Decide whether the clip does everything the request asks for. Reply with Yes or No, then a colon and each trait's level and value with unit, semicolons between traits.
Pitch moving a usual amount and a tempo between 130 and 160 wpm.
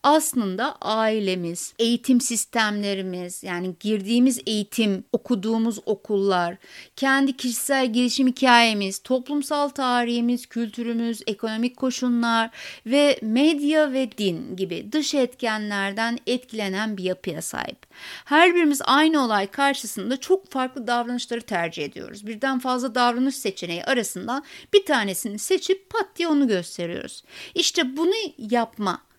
No: average, 4.3 semitones; average, 110 wpm